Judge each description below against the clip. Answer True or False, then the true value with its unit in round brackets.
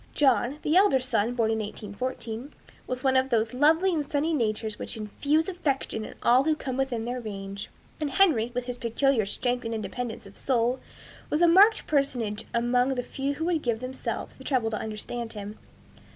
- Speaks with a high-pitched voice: True (250 Hz)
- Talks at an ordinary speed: True (190 wpm)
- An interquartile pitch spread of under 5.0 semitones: True (4.0 semitones)